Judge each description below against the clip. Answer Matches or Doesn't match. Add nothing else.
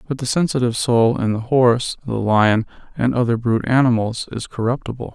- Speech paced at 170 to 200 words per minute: Matches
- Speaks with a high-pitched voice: Doesn't match